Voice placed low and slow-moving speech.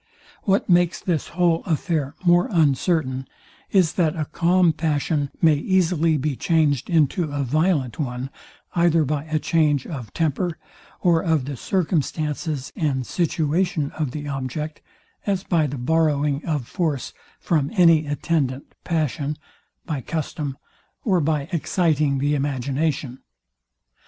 No: medium, 155 Hz; slow, 130 wpm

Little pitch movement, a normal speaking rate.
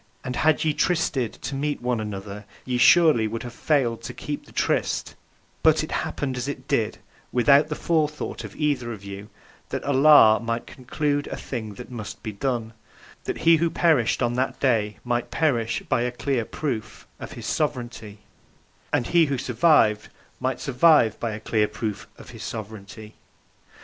No: average, 4.6 semitones; average, 175 wpm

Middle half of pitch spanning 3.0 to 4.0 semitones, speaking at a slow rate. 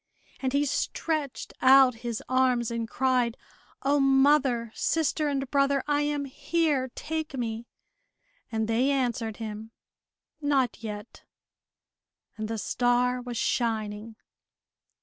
Yes: average, 3.5 semitones; slow, 115 wpm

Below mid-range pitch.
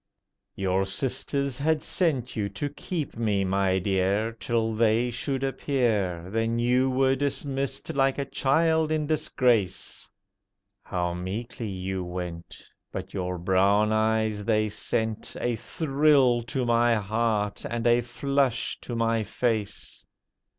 Yes: low, 115 Hz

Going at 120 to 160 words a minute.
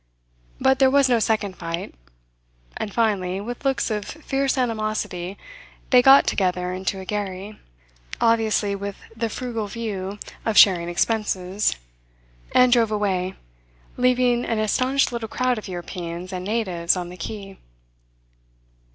Yes: slow, 135 wpm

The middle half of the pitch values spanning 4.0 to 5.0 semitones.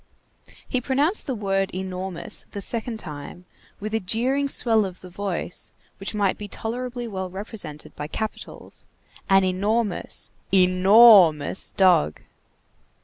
No: average, 3.5 semitones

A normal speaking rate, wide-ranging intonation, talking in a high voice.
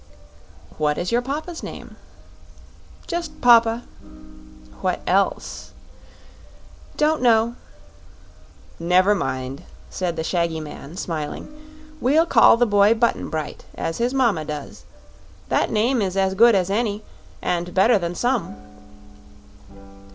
No: slow, 115 wpm; wide, 5.9 semitones; high, 205 Hz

